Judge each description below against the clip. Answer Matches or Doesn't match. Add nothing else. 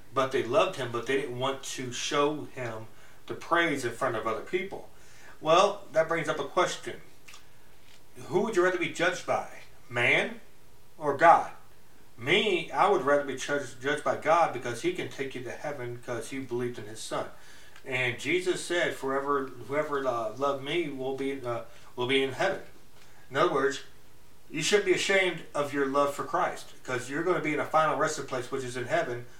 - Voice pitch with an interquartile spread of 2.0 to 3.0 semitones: Doesn't match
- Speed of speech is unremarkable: Matches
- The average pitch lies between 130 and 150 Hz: Matches